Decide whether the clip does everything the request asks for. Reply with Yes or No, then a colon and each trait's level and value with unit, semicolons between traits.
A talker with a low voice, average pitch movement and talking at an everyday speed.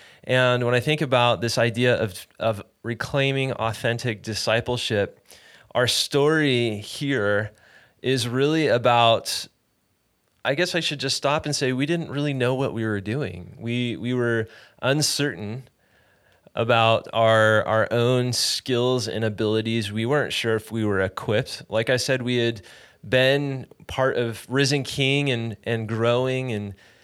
Yes: low, 120 Hz; average, 3.1 semitones; average, 145 wpm